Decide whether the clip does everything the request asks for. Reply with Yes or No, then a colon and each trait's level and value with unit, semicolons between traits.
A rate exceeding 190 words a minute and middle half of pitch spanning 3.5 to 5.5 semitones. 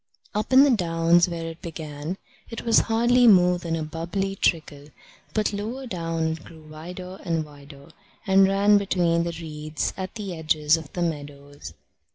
No: average, 170 wpm; average, 3.8 semitones